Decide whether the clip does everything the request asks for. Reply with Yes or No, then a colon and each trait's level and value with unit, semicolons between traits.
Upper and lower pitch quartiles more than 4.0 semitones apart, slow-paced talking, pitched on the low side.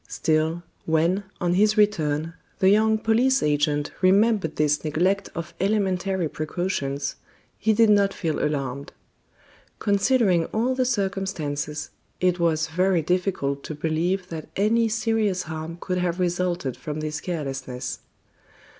No: average, 4.4 semitones; slow, 130 wpm; medium, 180 Hz